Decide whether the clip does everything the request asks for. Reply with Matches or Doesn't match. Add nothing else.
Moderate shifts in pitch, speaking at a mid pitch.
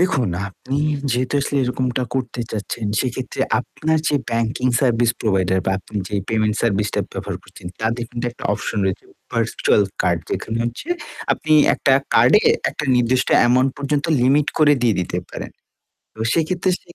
Doesn't match